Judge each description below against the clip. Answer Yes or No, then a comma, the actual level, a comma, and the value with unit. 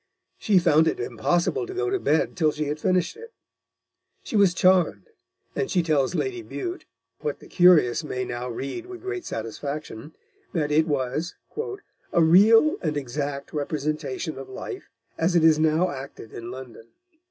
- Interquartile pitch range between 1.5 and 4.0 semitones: No, average, 5.1 semitones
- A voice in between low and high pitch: Yes, medium, 160 Hz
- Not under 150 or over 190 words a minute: Yes, average, 165 wpm